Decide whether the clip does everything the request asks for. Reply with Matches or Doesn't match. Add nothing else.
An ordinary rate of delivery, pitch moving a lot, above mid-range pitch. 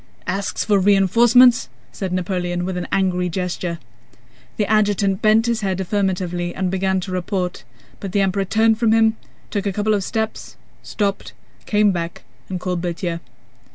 Doesn't match